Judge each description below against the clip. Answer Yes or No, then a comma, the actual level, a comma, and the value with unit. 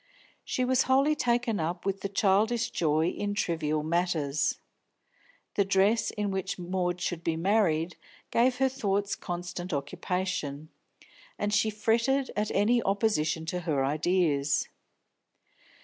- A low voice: No, high, 190 Hz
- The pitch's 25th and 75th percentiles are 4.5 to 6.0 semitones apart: Yes, average, 4.9 semitones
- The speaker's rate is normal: No, slow, 125 wpm